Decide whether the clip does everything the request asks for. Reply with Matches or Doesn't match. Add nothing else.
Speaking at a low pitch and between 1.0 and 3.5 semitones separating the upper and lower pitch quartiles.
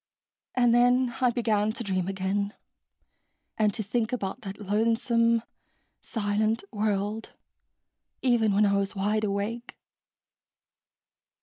Doesn't match